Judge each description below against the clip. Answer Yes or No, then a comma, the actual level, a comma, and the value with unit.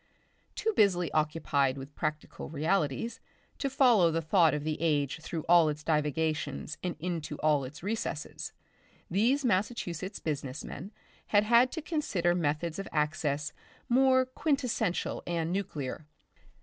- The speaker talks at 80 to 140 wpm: Yes, slow, 135 wpm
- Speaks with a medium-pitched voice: Yes, medium, 165 Hz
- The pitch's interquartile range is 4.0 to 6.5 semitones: Yes, wide, 5.5 semitones